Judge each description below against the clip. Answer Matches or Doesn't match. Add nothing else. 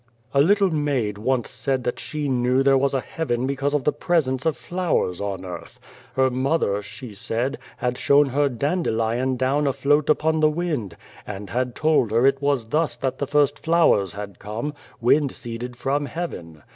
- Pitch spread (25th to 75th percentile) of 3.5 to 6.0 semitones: Matches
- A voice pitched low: Matches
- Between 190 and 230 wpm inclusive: Matches